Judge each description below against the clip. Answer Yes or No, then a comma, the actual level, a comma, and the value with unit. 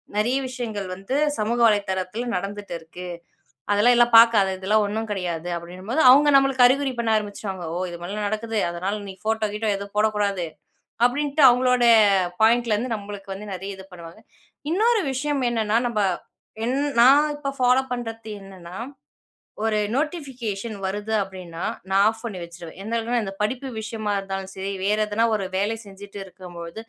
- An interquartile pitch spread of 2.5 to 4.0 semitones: Yes, average, 3.7 semitones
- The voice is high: Yes, high, 210 Hz